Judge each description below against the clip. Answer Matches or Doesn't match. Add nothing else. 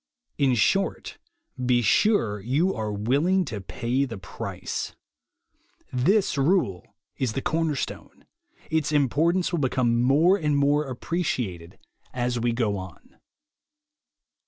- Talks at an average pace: Doesn't match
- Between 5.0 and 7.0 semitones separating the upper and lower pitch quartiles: Matches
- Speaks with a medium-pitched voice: Doesn't match